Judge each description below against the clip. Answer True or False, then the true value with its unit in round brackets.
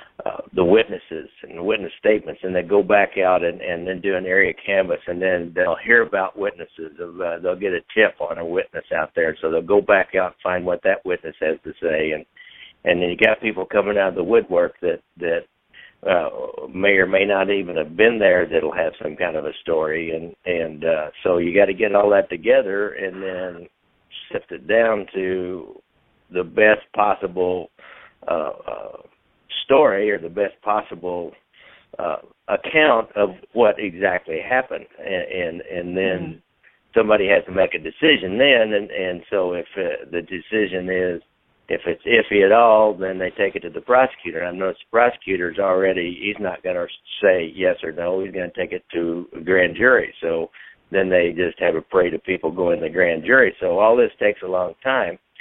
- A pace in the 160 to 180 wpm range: False (200 wpm)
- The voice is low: True (100 Hz)